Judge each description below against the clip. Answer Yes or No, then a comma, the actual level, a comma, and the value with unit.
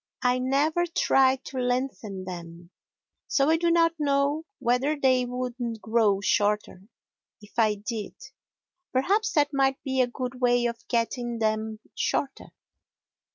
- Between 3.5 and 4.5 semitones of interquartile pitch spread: Yes, average, 4.0 semitones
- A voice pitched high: Yes, very high, 250 Hz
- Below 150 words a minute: Yes, slow, 135 wpm